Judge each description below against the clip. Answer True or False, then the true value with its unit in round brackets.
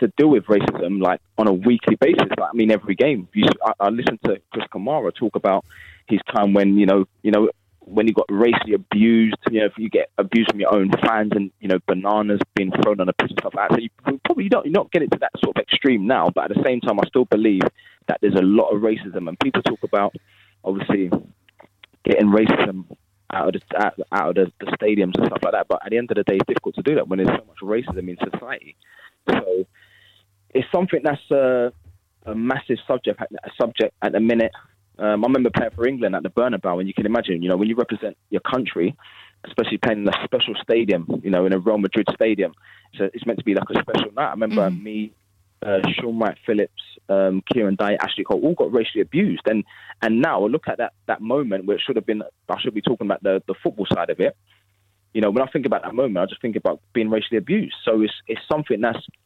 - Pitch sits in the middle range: False (105 Hz)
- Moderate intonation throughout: False (2.3 semitones)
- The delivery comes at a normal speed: False (245 wpm)